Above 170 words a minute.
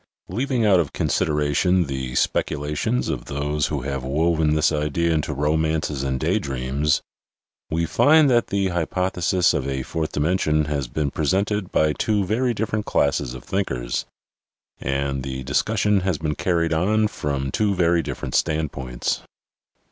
No: average, 150 wpm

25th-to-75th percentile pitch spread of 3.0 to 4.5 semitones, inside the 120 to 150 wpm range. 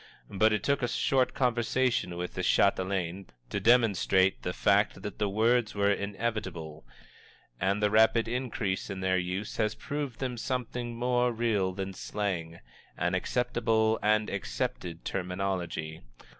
Yes: average, 4.1 semitones; average, 145 wpm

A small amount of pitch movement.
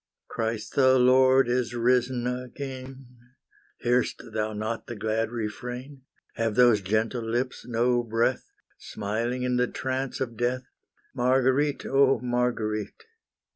Yes: narrow, 2.2 semitones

